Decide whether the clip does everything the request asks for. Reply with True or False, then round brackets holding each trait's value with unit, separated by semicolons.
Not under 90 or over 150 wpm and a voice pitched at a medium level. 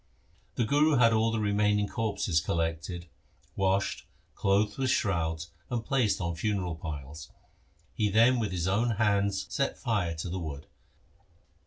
False (145 wpm; 100 Hz)